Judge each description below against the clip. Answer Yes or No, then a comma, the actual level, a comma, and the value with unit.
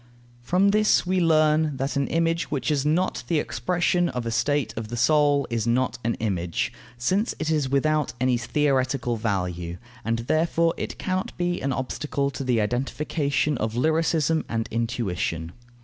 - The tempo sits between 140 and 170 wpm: Yes, average, 165 wpm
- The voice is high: No, medium, 140 Hz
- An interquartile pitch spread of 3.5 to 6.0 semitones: Yes, average, 5.2 semitones